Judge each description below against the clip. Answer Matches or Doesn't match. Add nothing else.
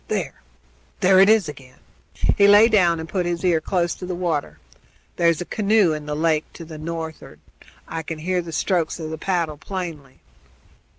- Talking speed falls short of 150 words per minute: Doesn't match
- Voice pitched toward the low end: Doesn't match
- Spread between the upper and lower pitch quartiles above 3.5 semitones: Doesn't match